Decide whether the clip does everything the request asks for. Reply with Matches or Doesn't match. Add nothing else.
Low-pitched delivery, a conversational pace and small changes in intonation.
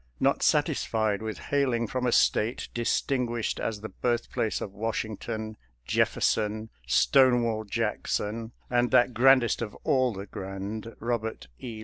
Doesn't match